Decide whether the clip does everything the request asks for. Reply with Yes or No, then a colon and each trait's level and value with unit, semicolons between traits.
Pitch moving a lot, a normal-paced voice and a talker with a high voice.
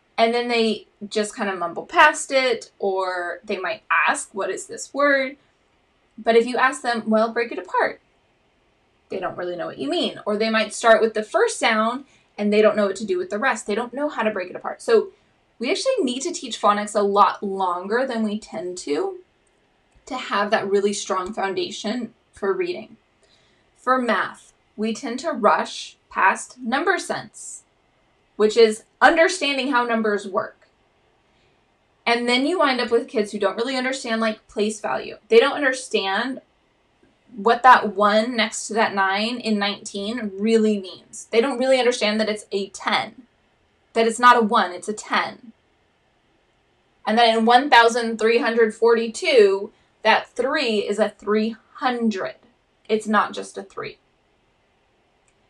No: average, 3.6 semitones; average, 165 wpm; high, 225 Hz